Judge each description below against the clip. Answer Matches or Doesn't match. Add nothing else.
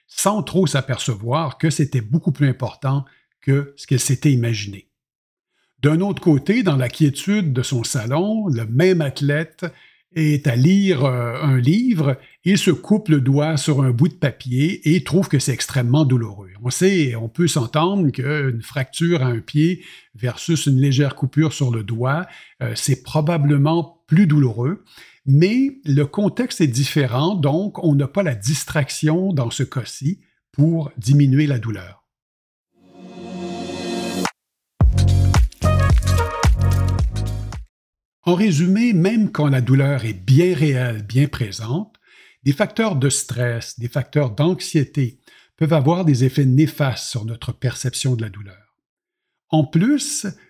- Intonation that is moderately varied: Matches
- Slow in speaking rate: Matches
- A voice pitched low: Doesn't match